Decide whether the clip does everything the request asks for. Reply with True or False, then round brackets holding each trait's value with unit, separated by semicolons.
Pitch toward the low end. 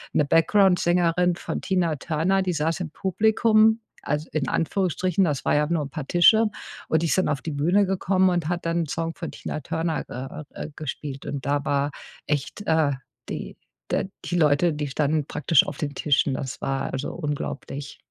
False (160 Hz)